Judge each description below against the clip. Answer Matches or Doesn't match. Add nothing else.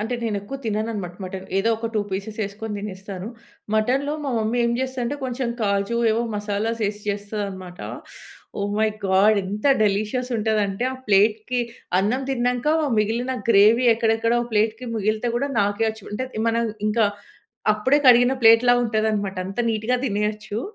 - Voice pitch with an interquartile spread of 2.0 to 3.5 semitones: Matches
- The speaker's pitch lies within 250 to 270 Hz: Doesn't match